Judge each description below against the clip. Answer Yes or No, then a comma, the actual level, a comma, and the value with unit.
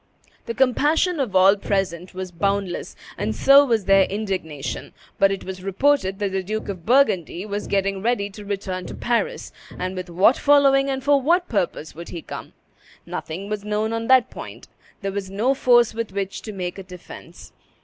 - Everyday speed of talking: Yes, average, 185 wpm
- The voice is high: Yes, high, 200 Hz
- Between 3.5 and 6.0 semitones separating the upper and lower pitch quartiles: Yes, average, 4.2 semitones